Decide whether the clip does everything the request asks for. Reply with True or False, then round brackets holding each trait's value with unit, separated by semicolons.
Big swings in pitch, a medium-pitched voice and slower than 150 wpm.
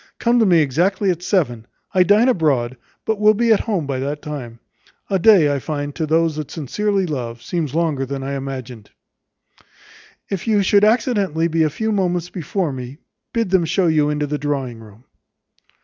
False (5.9 semitones; 160 Hz; 185 wpm)